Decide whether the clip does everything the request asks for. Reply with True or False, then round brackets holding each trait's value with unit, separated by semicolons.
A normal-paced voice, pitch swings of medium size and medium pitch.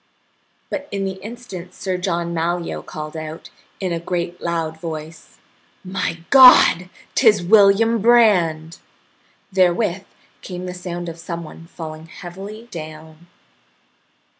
False (120 wpm; 3.0 semitones; 175 Hz)